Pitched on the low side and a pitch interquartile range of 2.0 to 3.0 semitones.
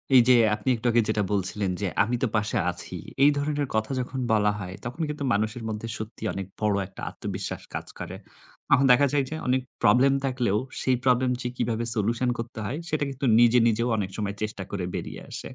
No: low, 115 Hz; average, 3.5 semitones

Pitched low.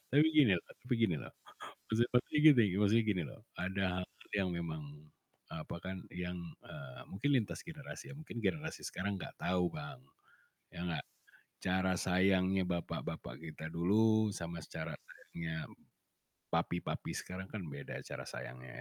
Yes: very low, 95 Hz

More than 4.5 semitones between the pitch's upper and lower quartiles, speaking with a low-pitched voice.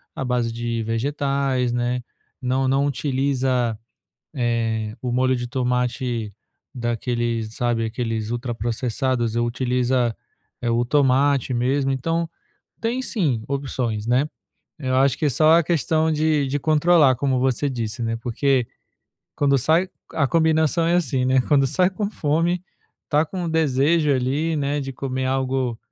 No: average, 3.3 semitones; low, 130 Hz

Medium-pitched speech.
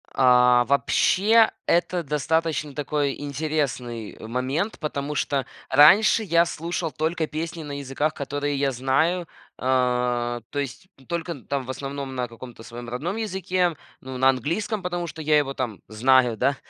Yes: medium, 145 Hz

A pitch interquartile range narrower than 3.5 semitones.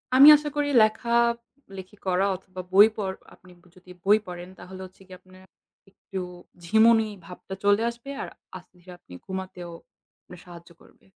Yes: average, 3.0 semitones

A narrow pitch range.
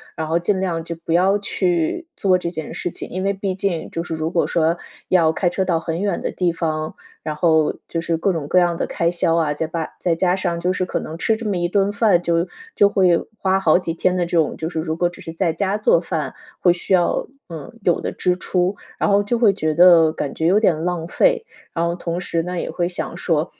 Yes: narrow, 2.3 semitones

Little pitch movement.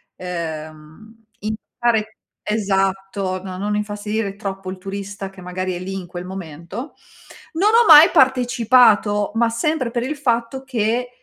No: average, 4.1 semitones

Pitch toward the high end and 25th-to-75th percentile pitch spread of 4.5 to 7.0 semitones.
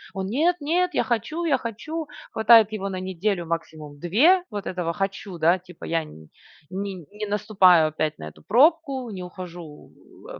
Yes: high, 195 Hz; wide, 5.5 semitones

